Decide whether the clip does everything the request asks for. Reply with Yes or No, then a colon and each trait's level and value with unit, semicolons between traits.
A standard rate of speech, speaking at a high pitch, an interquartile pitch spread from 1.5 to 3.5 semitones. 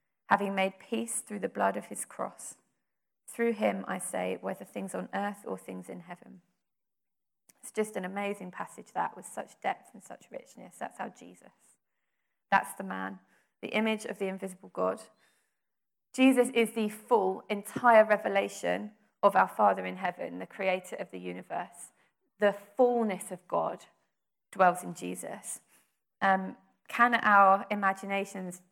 Yes: average, 150 wpm; high, 195 Hz; average, 3.2 semitones